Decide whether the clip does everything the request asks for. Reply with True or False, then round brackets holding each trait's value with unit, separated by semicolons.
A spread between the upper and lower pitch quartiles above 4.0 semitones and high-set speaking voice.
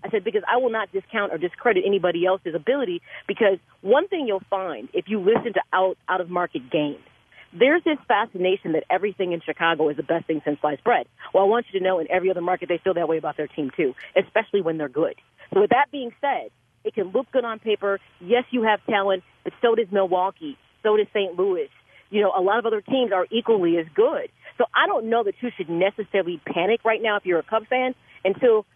True (4.6 semitones; 200 Hz)